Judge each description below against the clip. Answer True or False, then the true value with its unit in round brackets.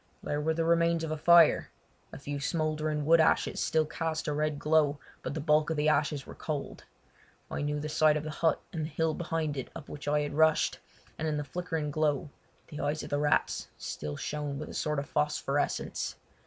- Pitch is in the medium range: True (150 Hz)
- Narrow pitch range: True (1.4 semitones)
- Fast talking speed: True (210 wpm)